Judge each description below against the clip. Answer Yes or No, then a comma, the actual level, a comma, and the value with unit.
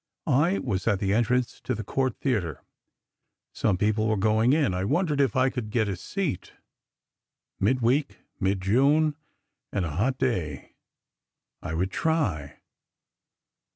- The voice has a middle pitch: No, low, 110 Hz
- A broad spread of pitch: Yes, wide, 5.8 semitones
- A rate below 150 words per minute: Yes, slow, 135 wpm